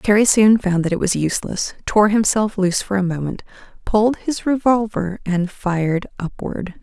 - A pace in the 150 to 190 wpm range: Yes, average, 165 wpm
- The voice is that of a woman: Yes, female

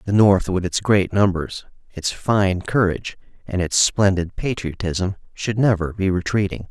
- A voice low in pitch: Yes, very low, 95 Hz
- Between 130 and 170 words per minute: Yes, average, 150 wpm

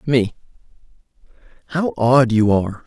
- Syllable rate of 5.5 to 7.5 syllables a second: No, 4.6 syllables/s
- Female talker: No, male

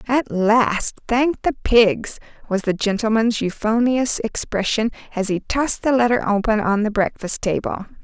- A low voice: No, high, 225 Hz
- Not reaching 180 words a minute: Yes, average, 150 wpm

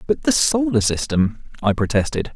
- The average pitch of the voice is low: Yes, low, 130 Hz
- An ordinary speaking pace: Yes, average, 155 wpm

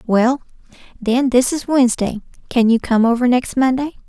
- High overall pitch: Yes, high, 245 Hz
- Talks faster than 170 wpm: No, average, 160 wpm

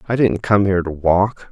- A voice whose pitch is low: Yes, very low, 95 Hz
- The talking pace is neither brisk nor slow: No, fast, 240 wpm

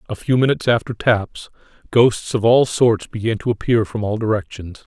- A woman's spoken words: No, male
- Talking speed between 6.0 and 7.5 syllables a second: No, 5.1 syllables/s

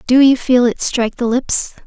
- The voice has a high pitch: Yes, very high, 250 Hz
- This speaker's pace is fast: Yes, fast, 225 wpm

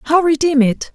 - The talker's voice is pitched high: Yes, very high, 295 Hz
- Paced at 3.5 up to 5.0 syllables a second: Yes, 4.4 syllables/s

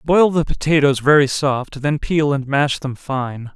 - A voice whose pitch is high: No, medium, 145 Hz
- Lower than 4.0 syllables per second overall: No, 4.1 syllables/s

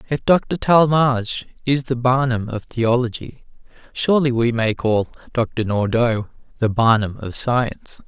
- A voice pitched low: Yes, low, 120 Hz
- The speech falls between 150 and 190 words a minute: No, slow, 135 wpm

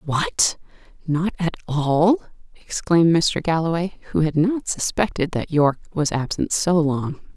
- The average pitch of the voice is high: No, medium, 165 Hz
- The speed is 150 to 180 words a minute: No, average, 140 wpm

